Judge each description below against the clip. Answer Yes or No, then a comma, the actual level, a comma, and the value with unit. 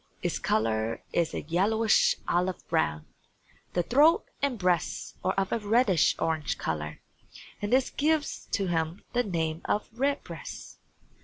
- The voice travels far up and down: Yes, wide, 6.7 semitones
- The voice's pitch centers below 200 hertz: Yes, medium, 185 Hz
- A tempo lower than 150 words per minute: Yes, average, 140 wpm